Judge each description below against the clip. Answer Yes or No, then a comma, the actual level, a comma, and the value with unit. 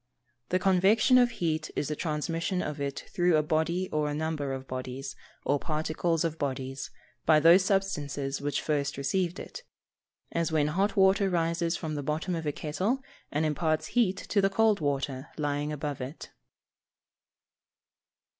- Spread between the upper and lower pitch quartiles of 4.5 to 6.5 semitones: No, average, 4.0 semitones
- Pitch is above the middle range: No, medium, 155 Hz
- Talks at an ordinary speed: Yes, average, 165 wpm